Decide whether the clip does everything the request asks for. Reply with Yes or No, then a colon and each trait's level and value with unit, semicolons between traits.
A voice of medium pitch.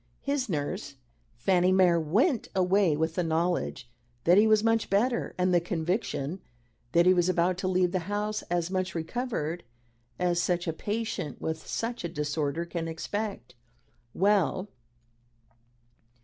Yes: medium, 180 Hz